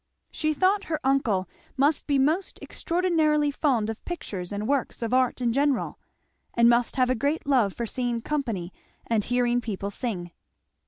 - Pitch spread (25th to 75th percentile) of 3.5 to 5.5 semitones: Yes, average, 4.5 semitones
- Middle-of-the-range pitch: No, very high, 255 Hz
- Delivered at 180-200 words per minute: No, average, 165 wpm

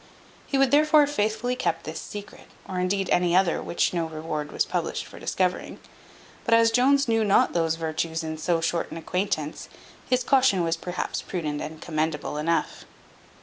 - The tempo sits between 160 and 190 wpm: Yes, average, 175 wpm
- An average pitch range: No, wide, 5.9 semitones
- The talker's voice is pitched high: No, medium, 180 Hz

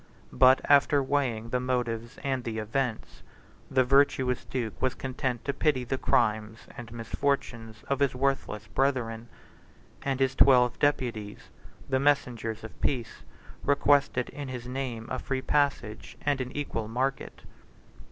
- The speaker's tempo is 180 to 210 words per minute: No, average, 140 wpm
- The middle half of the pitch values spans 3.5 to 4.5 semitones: No, average, 3.1 semitones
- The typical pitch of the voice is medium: No, low, 125 Hz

